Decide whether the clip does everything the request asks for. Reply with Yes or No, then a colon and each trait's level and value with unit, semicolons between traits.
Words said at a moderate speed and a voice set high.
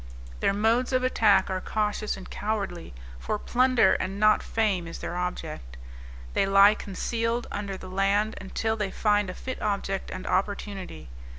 Yes: average, 160 wpm; high, 205 Hz